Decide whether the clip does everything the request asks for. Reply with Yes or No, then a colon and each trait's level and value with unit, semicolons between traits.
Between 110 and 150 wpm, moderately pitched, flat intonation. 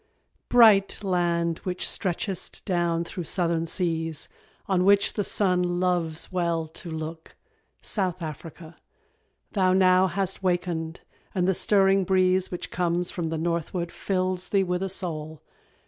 Yes: average, 140 wpm; medium, 180 Hz; narrow, 2.0 semitones